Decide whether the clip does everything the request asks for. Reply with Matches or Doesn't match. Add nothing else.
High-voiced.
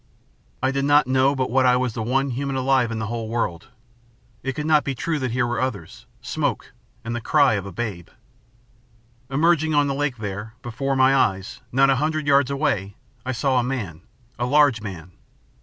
Doesn't match